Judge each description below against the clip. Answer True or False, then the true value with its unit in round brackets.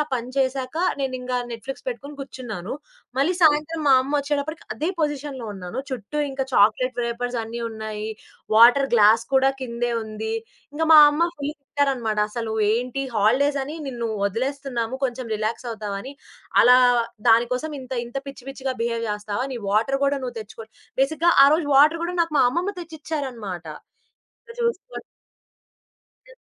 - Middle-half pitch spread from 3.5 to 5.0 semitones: True (3.9 semitones)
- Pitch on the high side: True (255 Hz)